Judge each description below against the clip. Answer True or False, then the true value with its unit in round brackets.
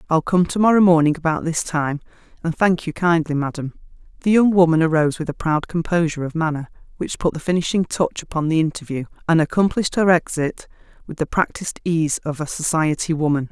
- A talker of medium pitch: True (165 Hz)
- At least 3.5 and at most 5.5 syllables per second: False (6.0 syllables/s)